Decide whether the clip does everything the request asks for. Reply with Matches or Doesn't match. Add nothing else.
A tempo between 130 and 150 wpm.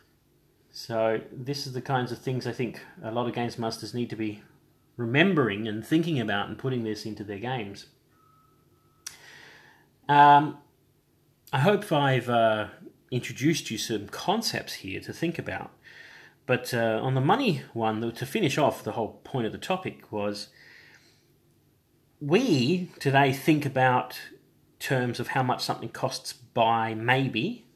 Matches